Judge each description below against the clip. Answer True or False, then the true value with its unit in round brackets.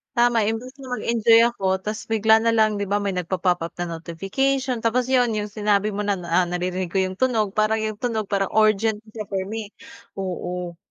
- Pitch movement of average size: True (3.0 semitones)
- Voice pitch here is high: True (210 Hz)